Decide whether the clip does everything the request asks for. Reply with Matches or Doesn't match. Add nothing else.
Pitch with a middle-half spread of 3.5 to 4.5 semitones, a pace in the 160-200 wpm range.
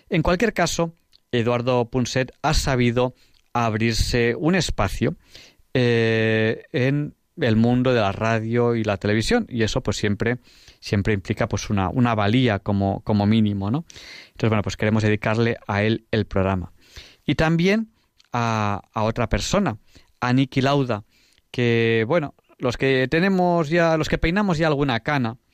Doesn't match